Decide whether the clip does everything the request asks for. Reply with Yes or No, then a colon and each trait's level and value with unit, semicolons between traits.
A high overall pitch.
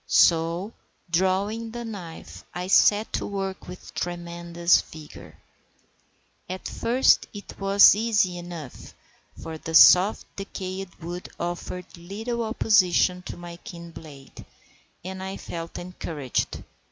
No: medium, 180 Hz